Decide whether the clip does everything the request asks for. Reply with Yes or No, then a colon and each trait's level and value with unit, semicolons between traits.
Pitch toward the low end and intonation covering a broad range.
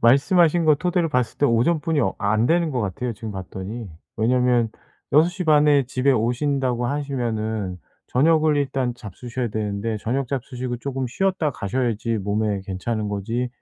No: low, 125 Hz; average, 4.6 semitones